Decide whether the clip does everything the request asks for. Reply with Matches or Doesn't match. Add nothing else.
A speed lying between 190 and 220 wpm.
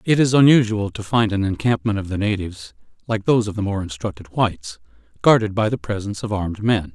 Matches